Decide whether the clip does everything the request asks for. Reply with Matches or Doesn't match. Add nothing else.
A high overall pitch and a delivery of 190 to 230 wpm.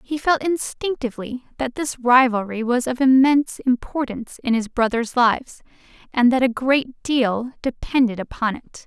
Doesn't match